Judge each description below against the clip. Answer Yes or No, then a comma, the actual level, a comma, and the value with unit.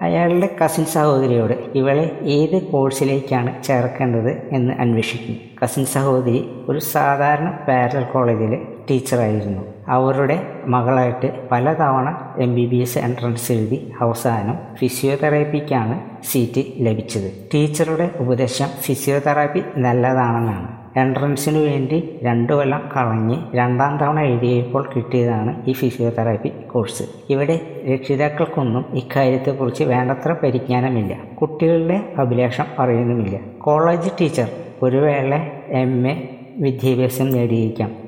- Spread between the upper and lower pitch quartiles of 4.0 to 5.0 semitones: No, average, 3.0 semitones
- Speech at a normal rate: Yes, average, 95 wpm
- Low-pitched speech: Yes, low, 130 Hz